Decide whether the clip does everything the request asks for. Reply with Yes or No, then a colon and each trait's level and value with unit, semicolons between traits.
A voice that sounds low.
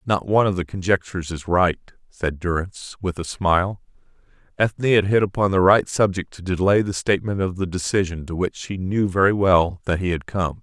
Yes: very low, 95 Hz